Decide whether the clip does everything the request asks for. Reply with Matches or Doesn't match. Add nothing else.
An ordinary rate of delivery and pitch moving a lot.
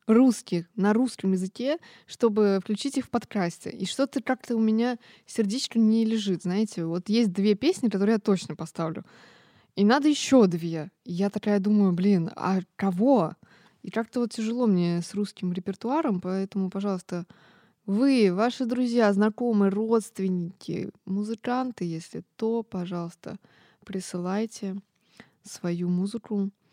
Doesn't match